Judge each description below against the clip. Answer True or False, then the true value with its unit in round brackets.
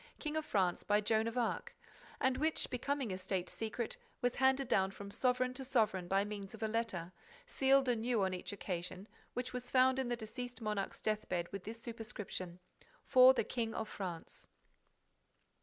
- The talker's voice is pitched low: False (225 Hz)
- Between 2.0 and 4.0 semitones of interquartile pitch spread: False (4.4 semitones)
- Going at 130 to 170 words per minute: False (180 wpm)